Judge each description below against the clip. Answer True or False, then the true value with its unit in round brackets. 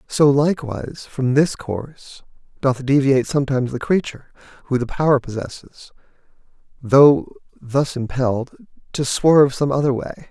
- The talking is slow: True (130 wpm)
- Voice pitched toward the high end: False (135 Hz)